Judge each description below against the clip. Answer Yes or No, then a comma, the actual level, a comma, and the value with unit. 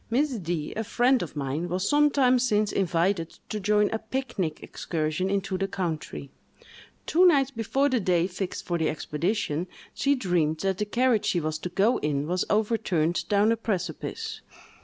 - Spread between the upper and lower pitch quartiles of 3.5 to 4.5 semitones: No, average, 5.2 semitones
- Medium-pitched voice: No, high, 195 Hz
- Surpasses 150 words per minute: Yes, average, 180 wpm